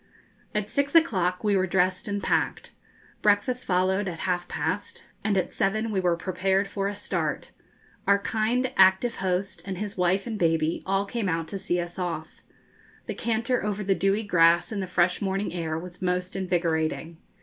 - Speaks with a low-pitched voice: No, high, 190 Hz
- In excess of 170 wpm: Yes, average, 180 wpm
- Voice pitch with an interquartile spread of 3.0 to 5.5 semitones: No, narrow, 2.6 semitones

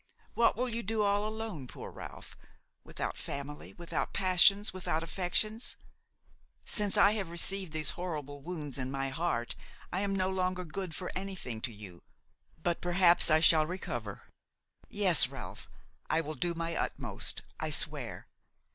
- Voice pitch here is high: No, medium, 175 Hz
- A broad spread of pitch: No, average, 4.3 semitones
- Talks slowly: No, average, 150 wpm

